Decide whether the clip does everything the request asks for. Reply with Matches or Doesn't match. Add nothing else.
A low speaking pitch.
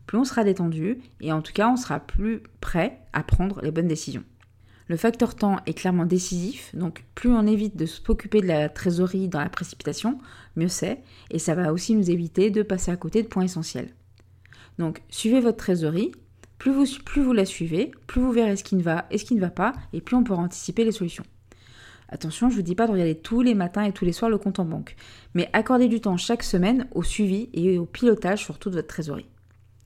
Doesn't match